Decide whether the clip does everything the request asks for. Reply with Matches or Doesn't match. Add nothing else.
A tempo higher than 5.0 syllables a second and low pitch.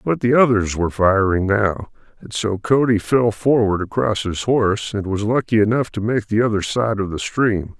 Doesn't match